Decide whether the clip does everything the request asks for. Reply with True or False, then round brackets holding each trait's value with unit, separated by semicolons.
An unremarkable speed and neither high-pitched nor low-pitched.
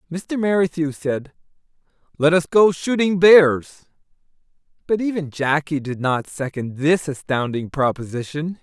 False (120 wpm; 155 Hz)